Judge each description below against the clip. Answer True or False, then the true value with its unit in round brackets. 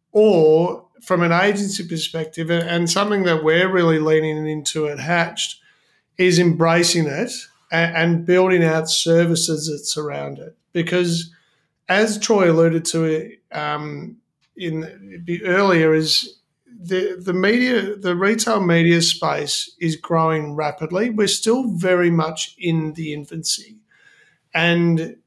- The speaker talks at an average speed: False (125 wpm)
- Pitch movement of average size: True (3.4 semitones)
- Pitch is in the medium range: True (170 Hz)